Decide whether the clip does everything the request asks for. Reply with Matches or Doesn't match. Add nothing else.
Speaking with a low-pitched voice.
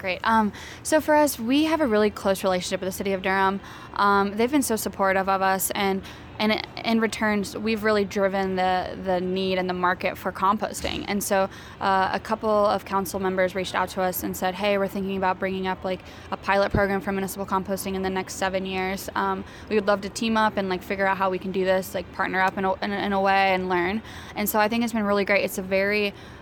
Doesn't match